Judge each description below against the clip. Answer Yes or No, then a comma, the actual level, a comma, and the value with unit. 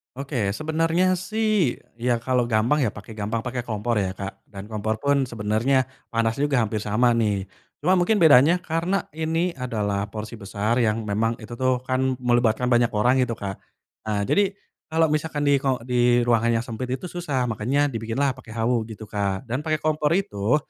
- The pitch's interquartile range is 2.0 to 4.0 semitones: No, average, 4.8 semitones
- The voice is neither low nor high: No, low, 120 Hz